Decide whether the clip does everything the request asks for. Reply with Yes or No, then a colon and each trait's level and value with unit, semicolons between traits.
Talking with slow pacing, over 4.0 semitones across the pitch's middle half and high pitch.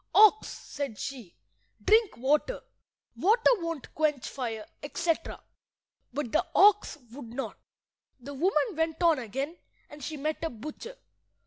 Yes: slow, 130 wpm; average, 4.4 semitones; very high, 300 Hz